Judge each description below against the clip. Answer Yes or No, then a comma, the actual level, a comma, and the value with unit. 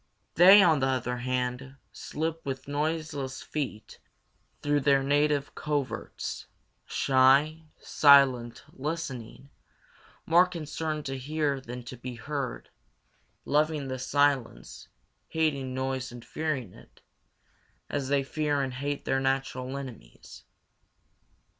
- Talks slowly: Yes, slow, 110 wpm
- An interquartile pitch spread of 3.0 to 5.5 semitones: No, narrow, 2.6 semitones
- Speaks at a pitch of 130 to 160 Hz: Yes, medium, 140 Hz